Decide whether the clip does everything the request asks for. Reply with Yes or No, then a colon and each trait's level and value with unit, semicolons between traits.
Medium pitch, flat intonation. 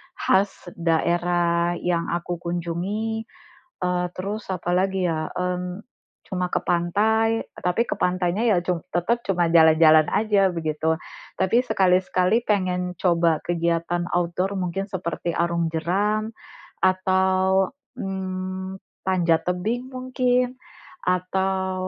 Yes: medium, 180 Hz; narrow, 2.1 semitones